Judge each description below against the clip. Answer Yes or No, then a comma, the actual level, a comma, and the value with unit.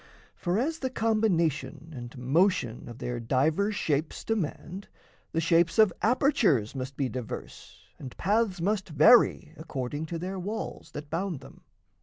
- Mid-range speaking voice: Yes, medium, 165 Hz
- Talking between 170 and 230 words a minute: No, average, 145 wpm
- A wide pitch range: Yes, wide, 6.8 semitones